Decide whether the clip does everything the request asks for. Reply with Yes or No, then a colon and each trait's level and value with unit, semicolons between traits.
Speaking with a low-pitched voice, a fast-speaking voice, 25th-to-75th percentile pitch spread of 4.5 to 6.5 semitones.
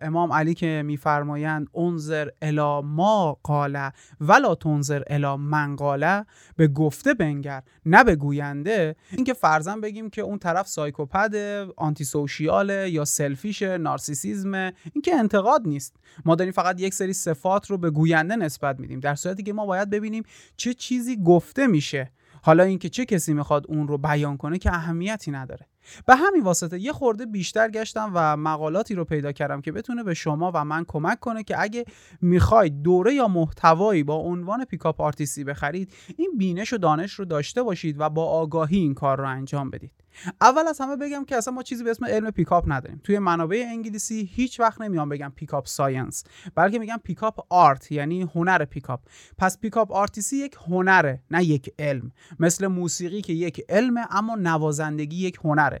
No: medium, 170 Hz; fast, 170 wpm; wide, 5.4 semitones